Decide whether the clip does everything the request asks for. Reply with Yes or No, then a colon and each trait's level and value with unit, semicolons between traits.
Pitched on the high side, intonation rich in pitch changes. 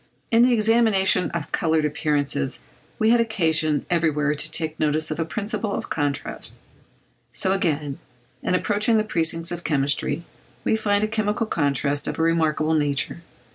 No: medium, 165 Hz; wide, 5.7 semitones